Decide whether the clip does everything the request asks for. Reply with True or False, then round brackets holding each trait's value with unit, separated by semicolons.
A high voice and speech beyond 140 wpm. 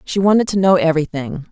False (175 Hz; 200 wpm)